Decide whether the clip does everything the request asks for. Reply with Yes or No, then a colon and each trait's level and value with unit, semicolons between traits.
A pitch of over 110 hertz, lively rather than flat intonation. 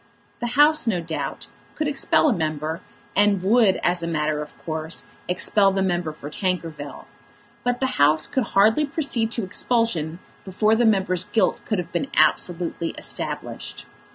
Yes: high, 190 Hz; wide, 5.8 semitones